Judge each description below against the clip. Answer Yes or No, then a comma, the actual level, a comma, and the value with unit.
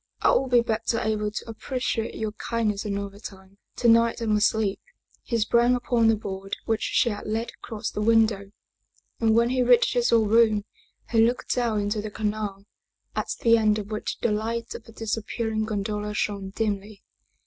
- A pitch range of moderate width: No, narrow, 1.7 semitones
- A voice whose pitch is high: Yes, high, 220 Hz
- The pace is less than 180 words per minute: No, average, 185 wpm